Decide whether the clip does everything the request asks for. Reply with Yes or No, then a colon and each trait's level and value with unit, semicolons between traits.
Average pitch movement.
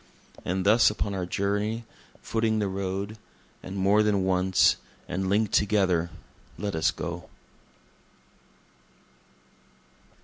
No: narrow, 2.1 semitones